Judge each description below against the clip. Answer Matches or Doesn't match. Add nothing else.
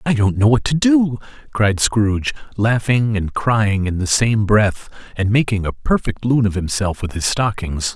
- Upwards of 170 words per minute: Matches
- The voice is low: Matches